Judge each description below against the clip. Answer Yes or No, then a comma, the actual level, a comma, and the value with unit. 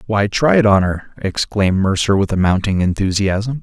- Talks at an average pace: Yes, average, 165 wpm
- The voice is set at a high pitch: No, low, 100 Hz